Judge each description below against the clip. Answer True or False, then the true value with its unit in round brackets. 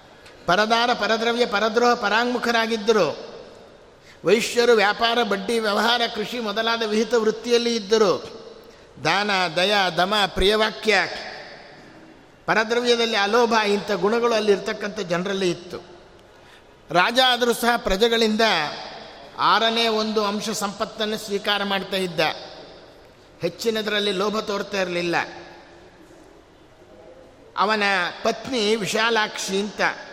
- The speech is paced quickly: False (85 wpm)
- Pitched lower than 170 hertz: False (215 Hz)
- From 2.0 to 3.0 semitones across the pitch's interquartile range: True (2.5 semitones)